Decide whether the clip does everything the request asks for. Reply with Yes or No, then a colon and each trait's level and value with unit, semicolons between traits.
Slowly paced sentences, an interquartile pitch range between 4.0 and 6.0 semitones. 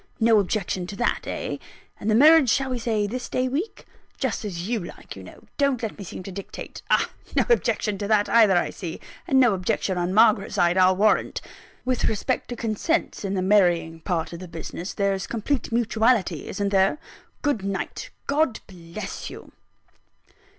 No: average, 185 wpm; average, 4.3 semitones